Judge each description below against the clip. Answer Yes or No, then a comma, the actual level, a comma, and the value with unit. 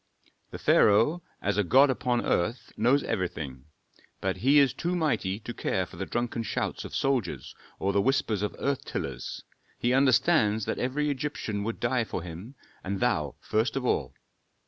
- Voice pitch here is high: No, low, 115 Hz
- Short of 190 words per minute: Yes, average, 170 wpm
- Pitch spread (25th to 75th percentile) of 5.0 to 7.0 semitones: Yes, wide, 5.4 semitones